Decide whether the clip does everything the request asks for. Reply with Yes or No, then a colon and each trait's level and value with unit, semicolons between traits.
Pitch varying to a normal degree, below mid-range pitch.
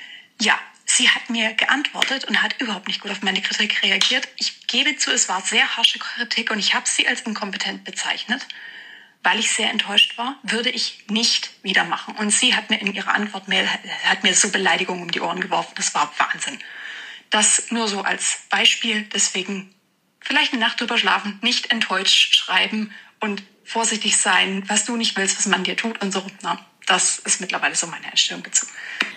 No: average, 3.1 semitones; high, 215 Hz